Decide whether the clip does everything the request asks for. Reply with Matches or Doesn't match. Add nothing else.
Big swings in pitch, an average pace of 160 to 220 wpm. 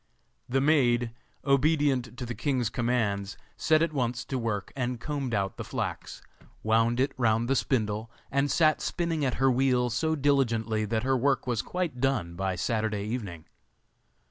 Doesn't match